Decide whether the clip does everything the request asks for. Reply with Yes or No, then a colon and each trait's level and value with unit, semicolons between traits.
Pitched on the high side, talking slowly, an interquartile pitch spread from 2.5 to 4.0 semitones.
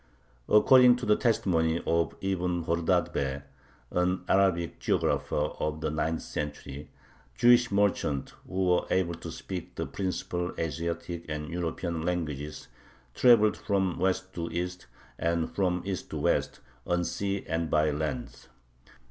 No: very low, 85 Hz; slow, 130 wpm; average, 2.9 semitones